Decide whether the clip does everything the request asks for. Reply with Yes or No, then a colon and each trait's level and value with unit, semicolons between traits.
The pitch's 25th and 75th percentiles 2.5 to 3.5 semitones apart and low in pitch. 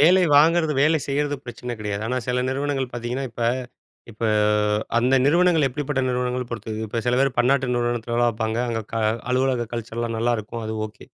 Yes: average, 2.9 semitones; low, 125 Hz